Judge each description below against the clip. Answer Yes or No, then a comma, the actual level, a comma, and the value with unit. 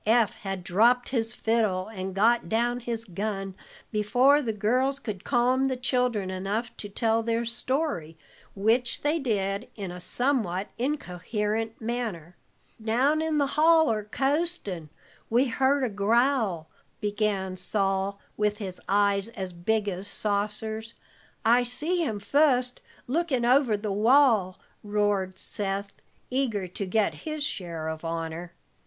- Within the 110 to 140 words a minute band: Yes, slow, 135 wpm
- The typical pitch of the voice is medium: No, high, 220 Hz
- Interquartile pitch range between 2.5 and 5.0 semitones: Yes, average, 4.2 semitones